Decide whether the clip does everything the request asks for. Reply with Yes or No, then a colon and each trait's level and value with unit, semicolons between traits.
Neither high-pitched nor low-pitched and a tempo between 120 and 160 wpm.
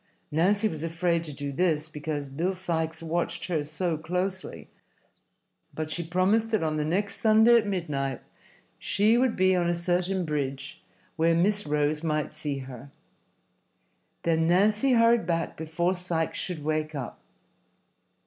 Yes: medium, 170 Hz; average, 150 wpm